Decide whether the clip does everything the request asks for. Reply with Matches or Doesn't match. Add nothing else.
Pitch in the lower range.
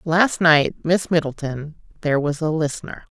Doesn't match